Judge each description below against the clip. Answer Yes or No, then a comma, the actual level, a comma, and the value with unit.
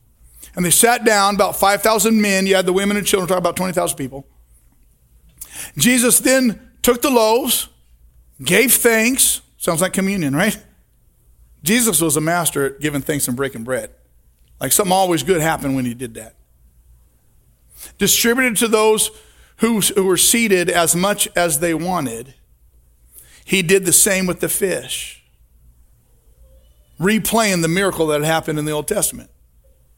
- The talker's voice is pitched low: No, medium, 175 Hz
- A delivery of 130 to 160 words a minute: Yes, average, 150 wpm